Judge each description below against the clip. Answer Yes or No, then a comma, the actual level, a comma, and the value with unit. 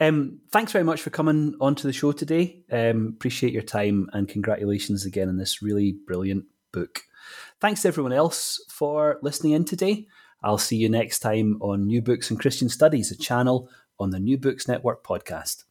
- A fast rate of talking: No, average, 185 wpm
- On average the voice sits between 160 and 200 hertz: No, low, 125 Hz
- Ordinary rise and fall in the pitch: No, wide, 6.5 semitones